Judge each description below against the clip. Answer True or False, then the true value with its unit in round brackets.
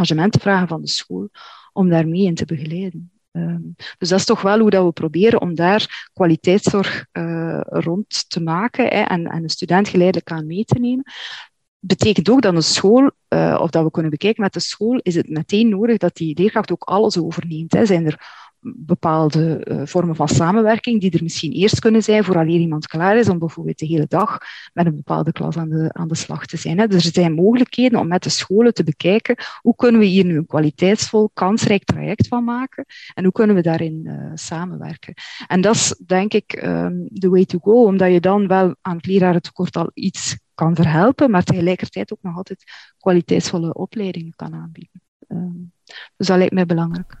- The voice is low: False (180 Hz)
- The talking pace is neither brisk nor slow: False (205 wpm)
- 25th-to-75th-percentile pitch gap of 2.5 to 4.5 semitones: True (3.7 semitones)